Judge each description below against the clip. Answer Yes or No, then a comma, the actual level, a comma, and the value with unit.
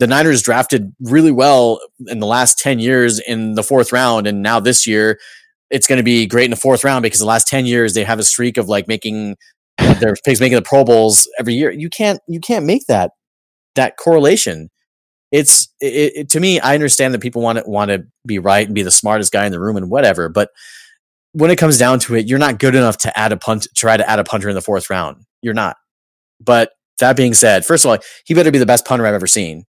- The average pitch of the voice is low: Yes, low, 120 Hz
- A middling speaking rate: No, fast, 245 wpm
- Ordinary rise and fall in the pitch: Yes, average, 3.6 semitones